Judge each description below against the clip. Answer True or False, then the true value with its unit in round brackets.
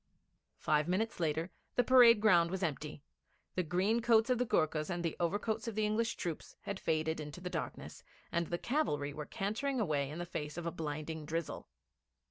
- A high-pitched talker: False (175 Hz)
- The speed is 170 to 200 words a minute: True (190 wpm)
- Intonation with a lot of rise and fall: True (5.8 semitones)